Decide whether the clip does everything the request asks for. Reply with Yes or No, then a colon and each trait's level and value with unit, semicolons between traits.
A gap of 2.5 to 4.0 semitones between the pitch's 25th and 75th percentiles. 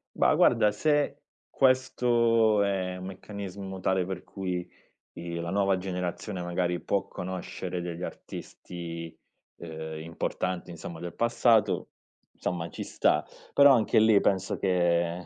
Yes: average, 2.8 semitones